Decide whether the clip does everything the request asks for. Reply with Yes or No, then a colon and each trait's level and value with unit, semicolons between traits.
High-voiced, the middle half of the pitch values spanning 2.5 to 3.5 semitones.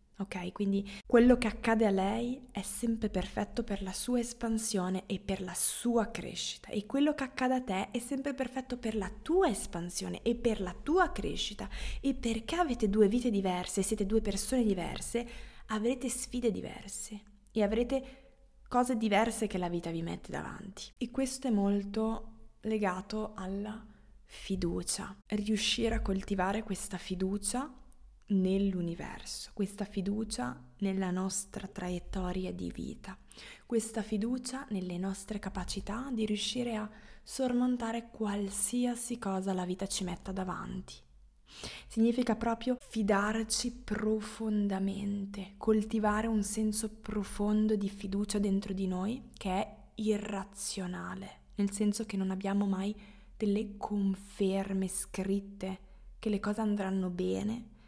Yes: high, 210 Hz; average, 2.9 semitones